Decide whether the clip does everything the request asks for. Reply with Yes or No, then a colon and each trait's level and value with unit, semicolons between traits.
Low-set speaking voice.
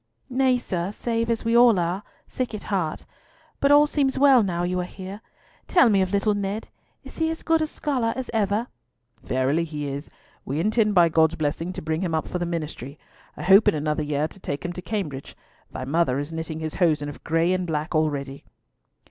No: medium, 180 Hz